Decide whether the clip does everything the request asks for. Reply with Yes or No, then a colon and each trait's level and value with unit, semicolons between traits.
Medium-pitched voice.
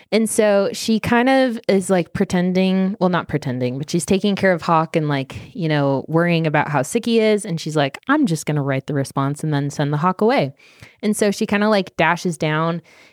Yes: medium, 175 Hz